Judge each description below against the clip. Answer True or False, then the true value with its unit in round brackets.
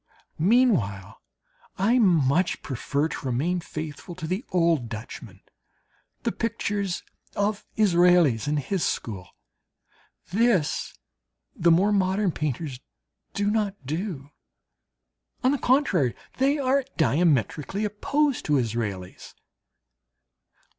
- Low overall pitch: False (175 Hz)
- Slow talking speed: True (100 wpm)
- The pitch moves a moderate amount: False (6.7 semitones)